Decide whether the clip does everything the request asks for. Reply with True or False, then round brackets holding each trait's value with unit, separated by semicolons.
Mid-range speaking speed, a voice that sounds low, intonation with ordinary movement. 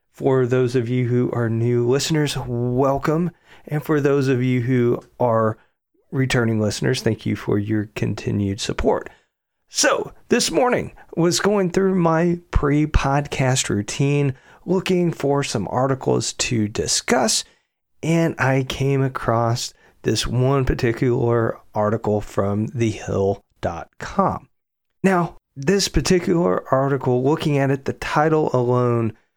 False (125 wpm; 130 Hz; 4.5 semitones)